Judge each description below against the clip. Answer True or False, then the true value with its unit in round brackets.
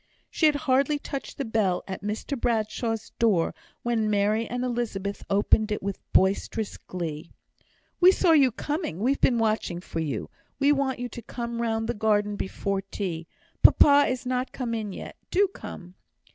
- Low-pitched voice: False (225 Hz)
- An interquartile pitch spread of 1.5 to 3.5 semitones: False (4.2 semitones)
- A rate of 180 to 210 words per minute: False (170 wpm)